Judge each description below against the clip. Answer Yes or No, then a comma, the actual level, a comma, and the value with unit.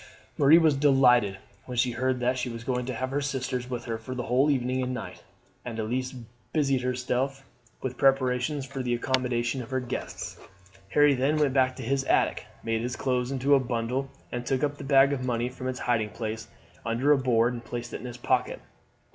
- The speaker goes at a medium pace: No, fast, 210 wpm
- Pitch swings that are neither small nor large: No, narrow, 1.9 semitones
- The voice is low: Yes, low, 130 Hz